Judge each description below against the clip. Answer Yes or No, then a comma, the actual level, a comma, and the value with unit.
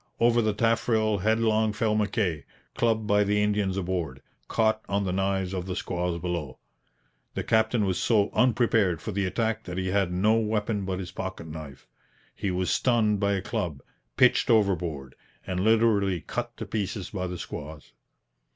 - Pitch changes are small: No, average, 3.4 semitones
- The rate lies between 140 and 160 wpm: No, average, 170 wpm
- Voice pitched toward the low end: Yes, low, 100 Hz